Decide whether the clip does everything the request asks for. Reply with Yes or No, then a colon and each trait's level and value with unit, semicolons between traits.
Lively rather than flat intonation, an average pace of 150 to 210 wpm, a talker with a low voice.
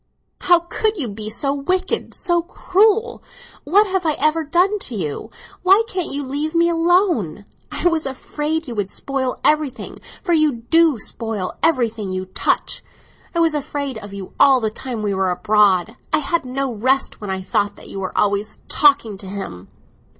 No: wide, 8.0 semitones; average, 180 wpm; very high, 275 Hz